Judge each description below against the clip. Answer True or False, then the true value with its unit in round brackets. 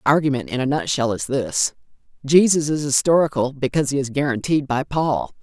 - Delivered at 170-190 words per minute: True (175 wpm)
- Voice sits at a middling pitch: True (145 Hz)